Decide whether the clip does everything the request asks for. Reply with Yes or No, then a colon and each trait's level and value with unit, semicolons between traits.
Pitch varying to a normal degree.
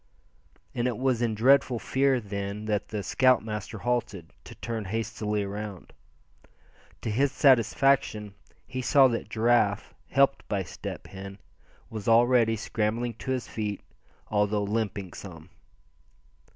Yes: average, 3.0 semitones